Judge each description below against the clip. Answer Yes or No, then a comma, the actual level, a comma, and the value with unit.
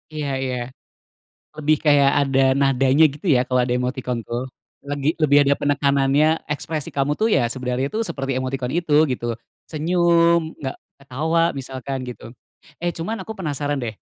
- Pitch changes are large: No, average, 3.2 semitones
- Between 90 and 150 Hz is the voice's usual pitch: Yes, medium, 140 Hz